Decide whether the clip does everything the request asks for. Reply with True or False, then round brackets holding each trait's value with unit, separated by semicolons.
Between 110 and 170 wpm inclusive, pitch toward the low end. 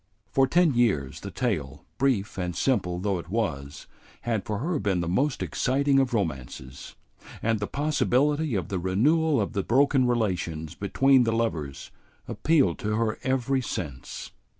True (155 wpm; 115 Hz)